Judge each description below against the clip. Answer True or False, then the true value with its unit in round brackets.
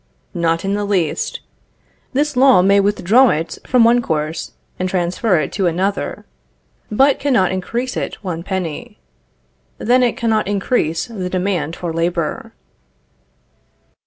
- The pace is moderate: False (130 wpm)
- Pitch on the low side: False (195 Hz)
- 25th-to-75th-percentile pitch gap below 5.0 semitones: False (5.3 semitones)